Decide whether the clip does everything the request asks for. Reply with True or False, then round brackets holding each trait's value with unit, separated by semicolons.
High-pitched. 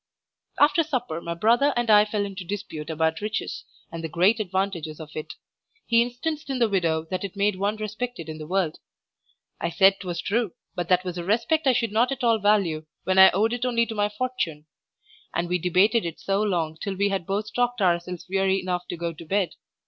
True (195 Hz)